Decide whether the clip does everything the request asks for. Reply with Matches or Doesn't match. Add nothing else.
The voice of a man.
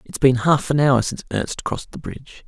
Matches